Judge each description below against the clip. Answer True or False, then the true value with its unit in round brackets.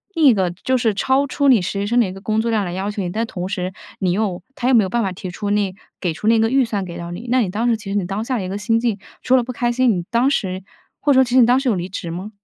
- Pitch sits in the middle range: False (215 Hz)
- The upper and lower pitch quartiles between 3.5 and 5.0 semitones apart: True (4.3 semitones)